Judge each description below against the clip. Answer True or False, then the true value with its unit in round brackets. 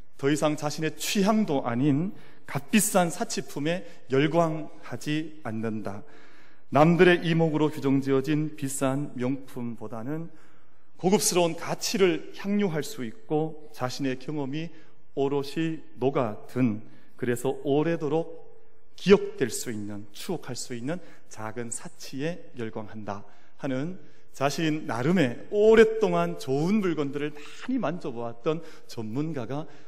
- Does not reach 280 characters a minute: True (255 characters per minute)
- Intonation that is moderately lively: True (4.0 semitones)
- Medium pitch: True (150 Hz)